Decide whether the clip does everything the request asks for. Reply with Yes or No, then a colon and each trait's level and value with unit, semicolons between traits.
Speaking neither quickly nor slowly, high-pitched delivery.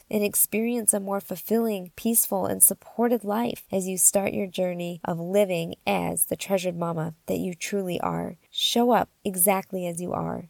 Yes: average, 170 wpm; high, 195 Hz